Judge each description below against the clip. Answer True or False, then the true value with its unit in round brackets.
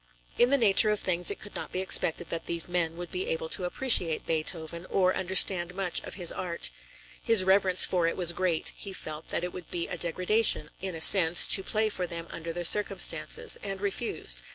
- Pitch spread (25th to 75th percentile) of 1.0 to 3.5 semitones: True (2.7 semitones)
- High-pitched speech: False (180 Hz)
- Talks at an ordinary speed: False (210 wpm)